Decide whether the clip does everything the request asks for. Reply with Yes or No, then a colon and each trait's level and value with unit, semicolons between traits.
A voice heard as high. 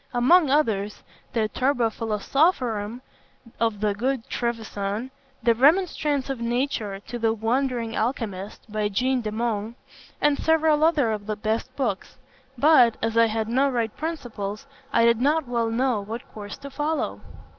Yes: high, 235 Hz